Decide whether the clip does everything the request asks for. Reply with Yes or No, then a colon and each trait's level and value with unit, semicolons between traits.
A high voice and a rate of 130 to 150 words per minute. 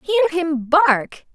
Yes: very high, 320 Hz; slow, 135 wpm